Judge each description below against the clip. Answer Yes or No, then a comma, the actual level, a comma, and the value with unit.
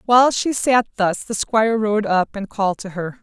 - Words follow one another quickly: Yes, fast, 225 wpm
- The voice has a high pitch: Yes, high, 215 Hz